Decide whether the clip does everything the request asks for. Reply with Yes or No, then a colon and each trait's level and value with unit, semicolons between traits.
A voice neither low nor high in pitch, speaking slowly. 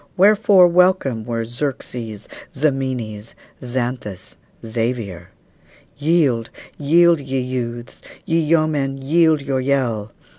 No: low, 130 Hz; slow, 90 wpm